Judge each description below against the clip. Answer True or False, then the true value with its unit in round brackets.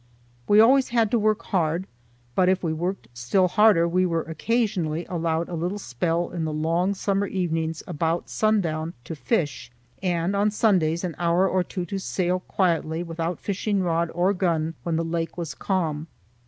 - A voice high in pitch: False (175 Hz)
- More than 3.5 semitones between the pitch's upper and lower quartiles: False (2.9 semitones)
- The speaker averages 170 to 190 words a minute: True (175 wpm)